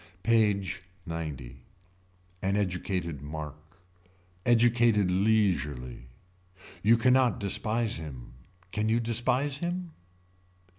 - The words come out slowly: Yes, slow, 90 wpm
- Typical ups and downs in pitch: No, wide, 6.8 semitones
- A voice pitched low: Yes, low, 100 Hz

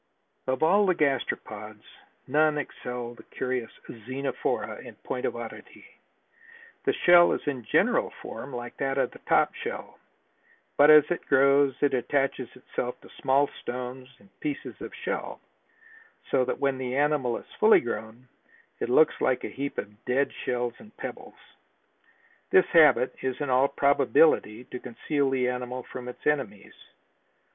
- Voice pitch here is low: Yes, low, 130 Hz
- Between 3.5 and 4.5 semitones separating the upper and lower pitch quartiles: No, average, 2.8 semitones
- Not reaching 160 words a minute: Yes, average, 150 wpm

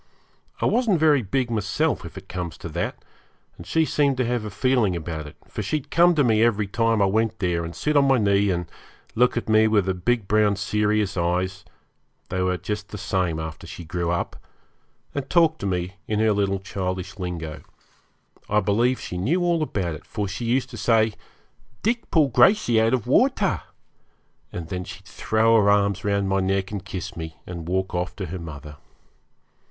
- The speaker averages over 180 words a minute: Yes, average, 200 wpm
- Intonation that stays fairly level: No, average, 4.5 semitones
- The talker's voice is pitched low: Yes, low, 100 Hz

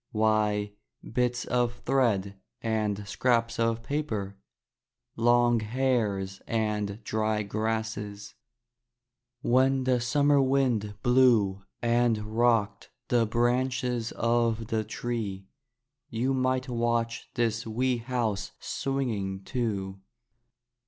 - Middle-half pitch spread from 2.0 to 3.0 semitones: Yes, narrow, 2.6 semitones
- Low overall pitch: Yes, low, 115 Hz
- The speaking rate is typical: No, slow, 95 wpm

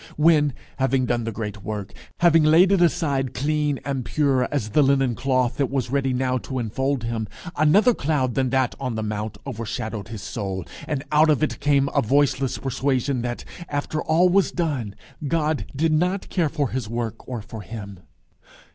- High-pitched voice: No, low, 135 Hz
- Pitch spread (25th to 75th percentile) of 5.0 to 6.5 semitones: No, average, 4.3 semitones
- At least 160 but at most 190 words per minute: Yes, average, 180 wpm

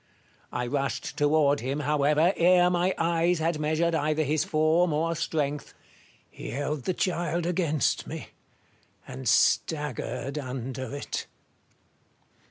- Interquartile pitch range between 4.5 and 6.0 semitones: No, average, 3.0 semitones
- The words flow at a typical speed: No, slow, 120 wpm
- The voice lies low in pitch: No, medium, 155 Hz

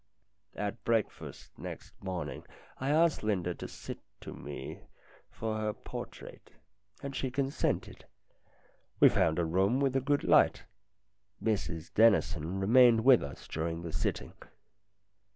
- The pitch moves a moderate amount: No, wide, 7.0 semitones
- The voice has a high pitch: No, low, 110 Hz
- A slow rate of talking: Yes, slow, 130 wpm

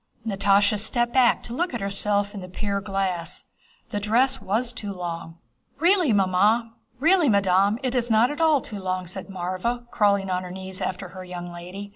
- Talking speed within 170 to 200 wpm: Yes, average, 175 wpm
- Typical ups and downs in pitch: Yes, average, 4.3 semitones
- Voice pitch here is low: No, high, 200 Hz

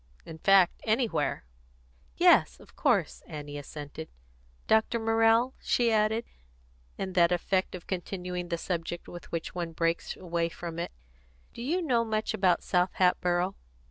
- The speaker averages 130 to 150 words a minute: Yes, average, 140 wpm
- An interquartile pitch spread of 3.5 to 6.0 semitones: Yes, average, 4.6 semitones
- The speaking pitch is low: No, medium, 180 Hz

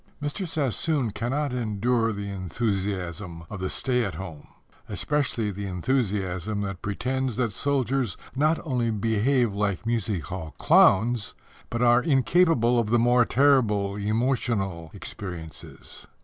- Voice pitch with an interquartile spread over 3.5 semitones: Yes, average, 4.4 semitones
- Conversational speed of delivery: No, slow, 125 wpm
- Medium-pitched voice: No, low, 115 Hz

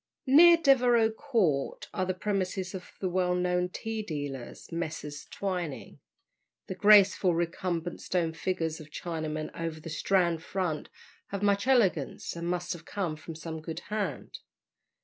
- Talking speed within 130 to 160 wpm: Yes, average, 145 wpm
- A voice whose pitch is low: No, medium, 180 Hz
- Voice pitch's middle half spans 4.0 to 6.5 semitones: No, average, 3.6 semitones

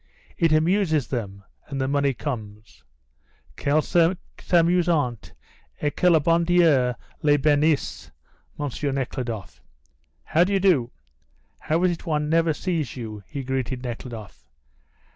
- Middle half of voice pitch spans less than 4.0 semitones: No, average, 5.0 semitones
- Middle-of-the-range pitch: Yes, medium, 145 Hz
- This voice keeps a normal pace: No, slow, 125 wpm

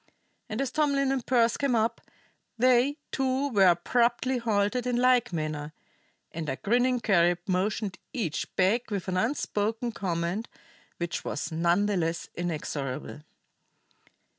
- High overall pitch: Yes, high, 215 Hz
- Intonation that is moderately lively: No, wide, 6.3 semitones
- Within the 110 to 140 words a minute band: Yes, slow, 135 wpm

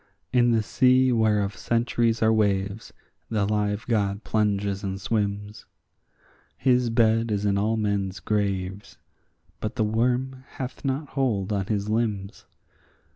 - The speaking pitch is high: No, low, 105 Hz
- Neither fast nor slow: No, slow, 130 wpm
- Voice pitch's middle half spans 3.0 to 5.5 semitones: No, narrow, 2.6 semitones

